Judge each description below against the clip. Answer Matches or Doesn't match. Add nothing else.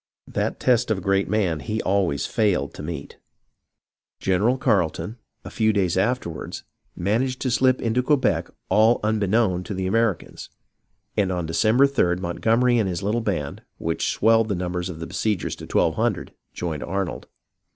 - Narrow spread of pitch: Doesn't match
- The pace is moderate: Matches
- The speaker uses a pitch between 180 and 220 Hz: Doesn't match